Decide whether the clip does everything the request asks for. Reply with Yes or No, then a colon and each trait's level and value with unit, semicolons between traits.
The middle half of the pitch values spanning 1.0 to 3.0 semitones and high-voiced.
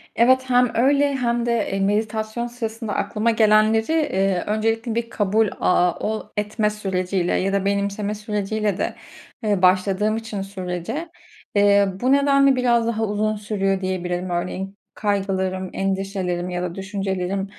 Yes: average, 2.7 semitones; high, 210 Hz